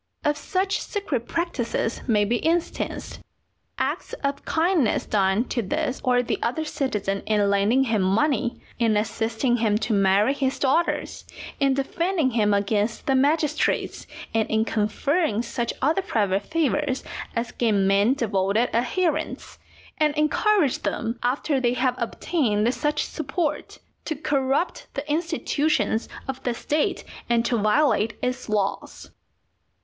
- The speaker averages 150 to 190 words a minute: No, slow, 135 wpm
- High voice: Yes, very high, 250 Hz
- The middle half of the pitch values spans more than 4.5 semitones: Yes, wide, 5.4 semitones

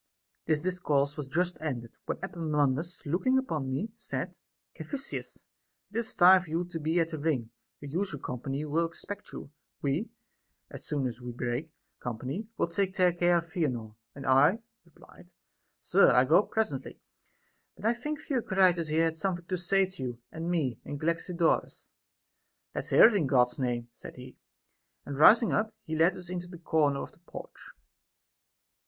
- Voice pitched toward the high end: No, medium, 165 Hz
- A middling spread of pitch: Yes, average, 4.7 semitones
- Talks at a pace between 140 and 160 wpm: No, average, 170 wpm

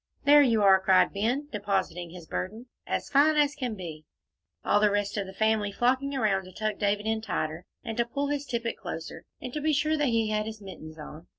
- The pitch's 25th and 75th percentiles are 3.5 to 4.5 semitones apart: No, average, 5.0 semitones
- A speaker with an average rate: No, fast, 220 wpm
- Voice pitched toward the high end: Yes, high, 215 Hz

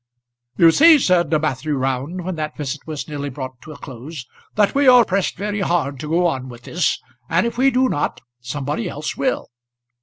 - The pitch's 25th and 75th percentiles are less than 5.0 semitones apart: No, wide, 5.5 semitones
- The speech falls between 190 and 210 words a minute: Yes, average, 195 wpm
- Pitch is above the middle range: No, medium, 155 Hz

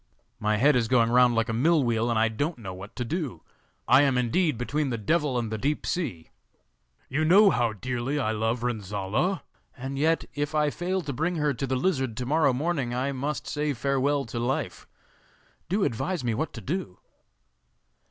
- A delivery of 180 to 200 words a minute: Yes, average, 195 wpm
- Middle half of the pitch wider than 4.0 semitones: Yes, average, 4.4 semitones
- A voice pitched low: Yes, low, 130 Hz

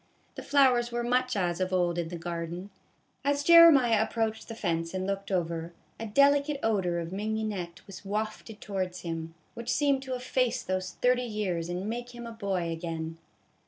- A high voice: Yes, high, 205 Hz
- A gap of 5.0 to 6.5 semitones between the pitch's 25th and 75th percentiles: Yes, wide, 5.6 semitones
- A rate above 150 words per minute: Yes, average, 180 wpm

